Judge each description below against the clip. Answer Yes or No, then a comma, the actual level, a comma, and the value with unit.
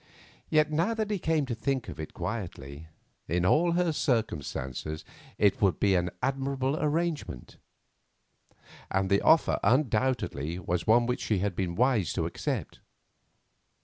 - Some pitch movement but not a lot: No, wide, 8.7 semitones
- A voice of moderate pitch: No, low, 115 Hz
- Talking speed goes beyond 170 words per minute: No, average, 145 wpm